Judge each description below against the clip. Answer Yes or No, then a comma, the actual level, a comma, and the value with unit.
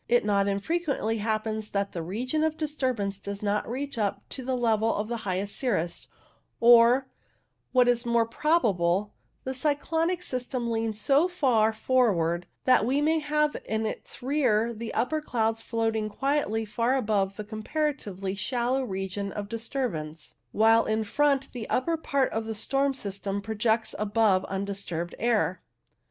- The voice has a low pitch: No, high, 225 Hz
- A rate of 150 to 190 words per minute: Yes, average, 155 wpm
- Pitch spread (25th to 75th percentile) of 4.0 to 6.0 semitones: Yes, average, 4.3 semitones